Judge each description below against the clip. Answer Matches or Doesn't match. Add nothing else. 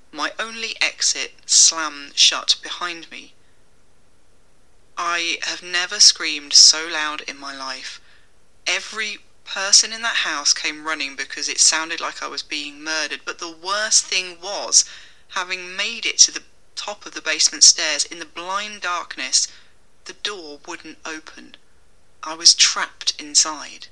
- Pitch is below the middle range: Doesn't match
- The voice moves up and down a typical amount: Matches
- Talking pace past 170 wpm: Doesn't match